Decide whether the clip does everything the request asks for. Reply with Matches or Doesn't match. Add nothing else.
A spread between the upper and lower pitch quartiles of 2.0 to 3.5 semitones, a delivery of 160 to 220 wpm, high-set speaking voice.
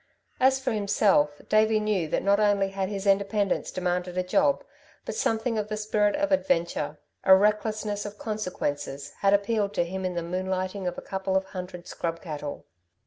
Matches